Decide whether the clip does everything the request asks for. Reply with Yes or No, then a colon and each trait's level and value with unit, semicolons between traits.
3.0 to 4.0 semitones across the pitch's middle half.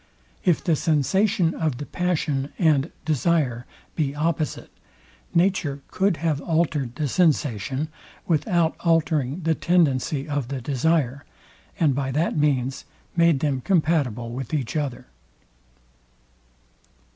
Yes: average, 3.6 semitones